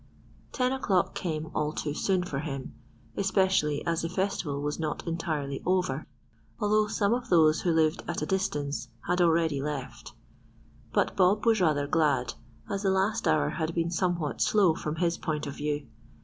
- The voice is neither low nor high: Yes, medium, 165 Hz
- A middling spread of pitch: Yes, average, 4.0 semitones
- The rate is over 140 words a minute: Yes, average, 170 wpm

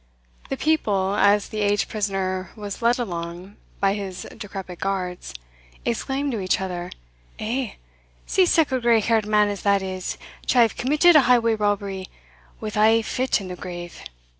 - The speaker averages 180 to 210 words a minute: No, average, 165 wpm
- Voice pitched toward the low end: No, high, 205 Hz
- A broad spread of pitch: No, average, 3.6 semitones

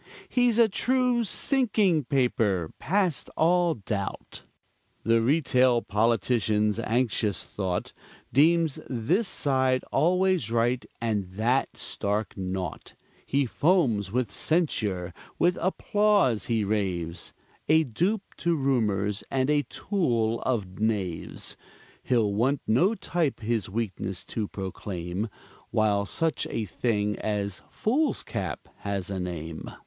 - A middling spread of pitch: No, wide, 7.9 semitones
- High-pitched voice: No, low, 115 Hz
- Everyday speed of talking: No, slow, 115 wpm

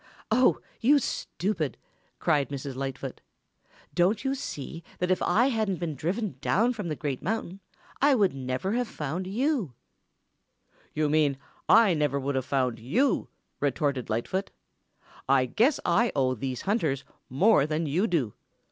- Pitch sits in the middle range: Yes, medium, 165 Hz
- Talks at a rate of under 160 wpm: Yes, average, 150 wpm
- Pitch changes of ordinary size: No, wide, 7.9 semitones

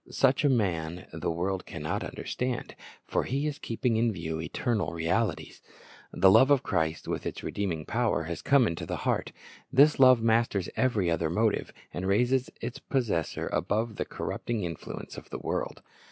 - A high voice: No, low, 110 Hz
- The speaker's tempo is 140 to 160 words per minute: No, average, 170 wpm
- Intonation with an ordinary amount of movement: No, wide, 6.5 semitones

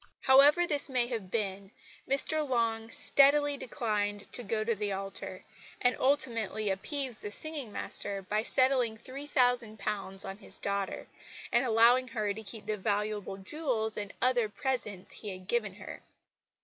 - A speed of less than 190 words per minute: Yes, average, 150 wpm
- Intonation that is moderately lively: Yes, average, 4.0 semitones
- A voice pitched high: Yes, high, 225 Hz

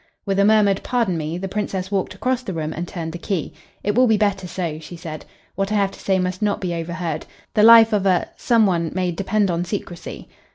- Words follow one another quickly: Yes, fast, 235 wpm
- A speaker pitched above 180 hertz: Yes, high, 190 Hz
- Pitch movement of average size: Yes, average, 3.3 semitones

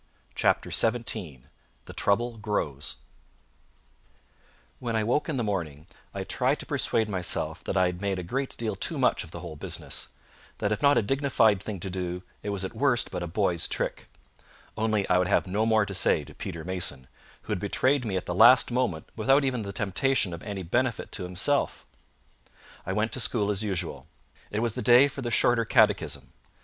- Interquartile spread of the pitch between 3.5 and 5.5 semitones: Yes, average, 4.6 semitones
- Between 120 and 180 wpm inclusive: No, average, 195 wpm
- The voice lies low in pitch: Yes, low, 105 Hz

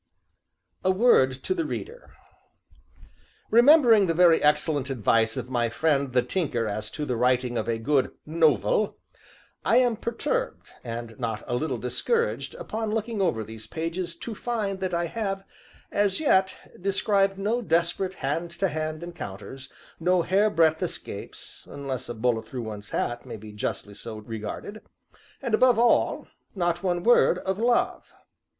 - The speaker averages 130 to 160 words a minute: Yes, average, 155 wpm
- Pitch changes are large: Yes, wide, 8.7 semitones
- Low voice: No, medium, 165 Hz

